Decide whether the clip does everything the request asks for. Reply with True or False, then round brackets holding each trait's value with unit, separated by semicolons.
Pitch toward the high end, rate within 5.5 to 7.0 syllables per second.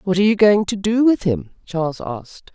True (195 Hz; 5.6 syllables/s)